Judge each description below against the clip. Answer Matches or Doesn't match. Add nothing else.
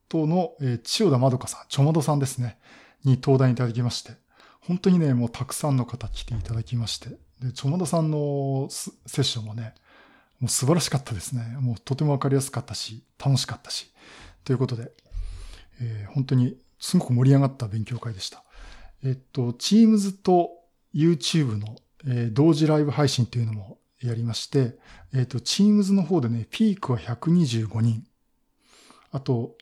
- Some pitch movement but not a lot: Matches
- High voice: Doesn't match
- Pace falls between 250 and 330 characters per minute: Doesn't match